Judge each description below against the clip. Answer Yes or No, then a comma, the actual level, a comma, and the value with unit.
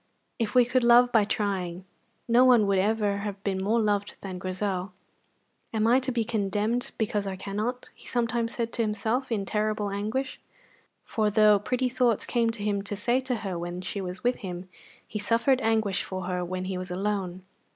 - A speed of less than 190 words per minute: No, average, 195 wpm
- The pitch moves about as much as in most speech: Yes, average, 3.2 semitones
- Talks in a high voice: Yes, high, 210 Hz